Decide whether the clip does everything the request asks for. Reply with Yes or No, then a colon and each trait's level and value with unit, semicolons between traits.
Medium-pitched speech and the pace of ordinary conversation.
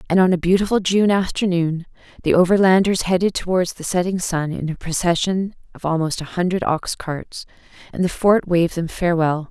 Yes: medium, 175 Hz; average, 175 wpm